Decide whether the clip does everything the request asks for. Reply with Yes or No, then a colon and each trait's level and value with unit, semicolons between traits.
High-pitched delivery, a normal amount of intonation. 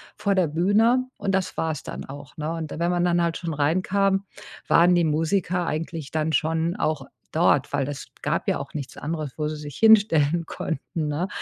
No: medium, 165 Hz; average, 3.1 semitones